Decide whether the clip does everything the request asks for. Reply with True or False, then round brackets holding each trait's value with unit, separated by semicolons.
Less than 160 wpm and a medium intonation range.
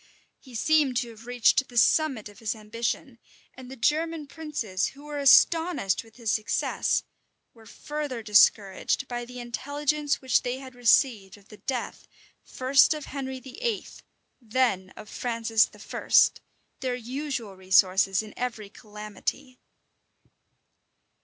True (135 wpm; 4.3 semitones)